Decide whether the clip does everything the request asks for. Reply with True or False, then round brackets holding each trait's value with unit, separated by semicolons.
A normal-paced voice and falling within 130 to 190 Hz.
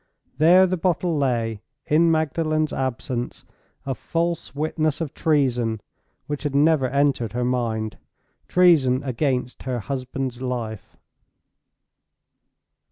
False (100 wpm; 135 Hz)